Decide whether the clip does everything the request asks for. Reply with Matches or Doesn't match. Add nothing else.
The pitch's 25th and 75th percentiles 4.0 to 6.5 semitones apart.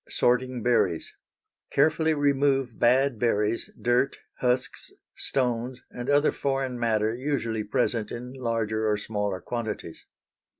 Doesn't match